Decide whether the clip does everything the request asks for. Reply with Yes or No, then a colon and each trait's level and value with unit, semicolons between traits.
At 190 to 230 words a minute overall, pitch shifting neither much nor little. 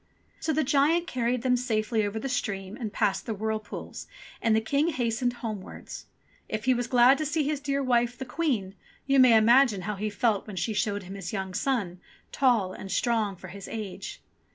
Yes: average, 200 wpm; average, 4.0 semitones